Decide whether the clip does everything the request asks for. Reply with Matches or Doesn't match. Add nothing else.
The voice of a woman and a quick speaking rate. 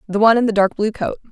Matches